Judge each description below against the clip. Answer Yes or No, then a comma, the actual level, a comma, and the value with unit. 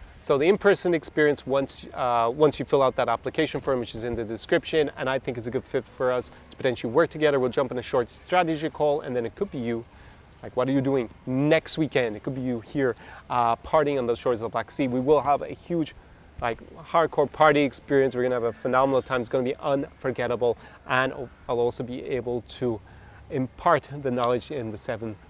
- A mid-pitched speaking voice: No, low, 130 Hz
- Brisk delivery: Yes, fast, 235 wpm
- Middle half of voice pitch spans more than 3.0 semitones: Yes, average, 3.5 semitones